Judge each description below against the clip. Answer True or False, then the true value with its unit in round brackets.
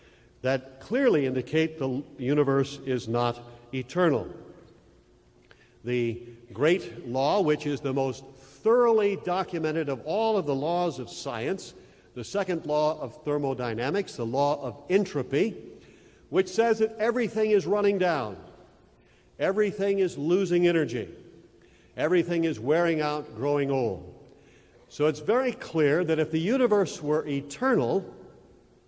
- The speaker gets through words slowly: True (125 wpm)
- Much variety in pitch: True (5.9 semitones)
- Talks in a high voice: False (150 Hz)